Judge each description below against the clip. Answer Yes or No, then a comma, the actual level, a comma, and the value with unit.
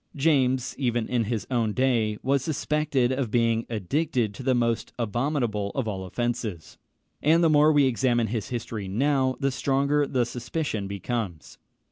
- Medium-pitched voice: No, low, 120 Hz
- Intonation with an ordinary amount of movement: Yes, average, 3.7 semitones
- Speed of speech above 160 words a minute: No, average, 155 wpm